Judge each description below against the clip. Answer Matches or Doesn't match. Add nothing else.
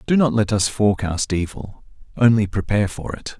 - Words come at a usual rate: Matches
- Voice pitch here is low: Matches